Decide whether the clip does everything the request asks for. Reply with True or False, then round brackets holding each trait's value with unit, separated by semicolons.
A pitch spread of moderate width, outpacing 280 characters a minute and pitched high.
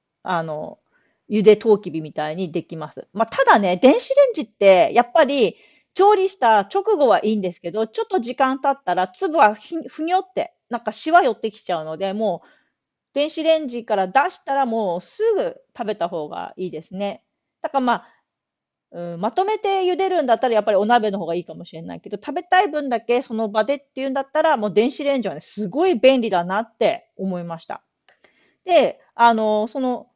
False (7.0 semitones; 380 characters per minute; 235 Hz)